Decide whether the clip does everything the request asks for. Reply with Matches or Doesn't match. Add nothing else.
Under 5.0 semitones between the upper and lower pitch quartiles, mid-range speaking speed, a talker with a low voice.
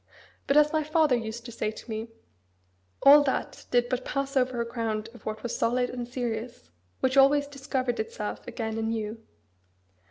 Doesn't match